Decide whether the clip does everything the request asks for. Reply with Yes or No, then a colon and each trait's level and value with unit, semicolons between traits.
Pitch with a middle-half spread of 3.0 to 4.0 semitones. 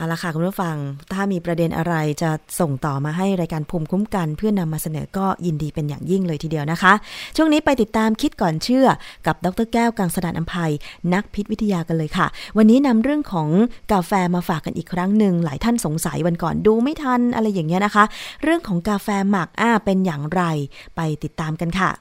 No: average, 4.4 semitones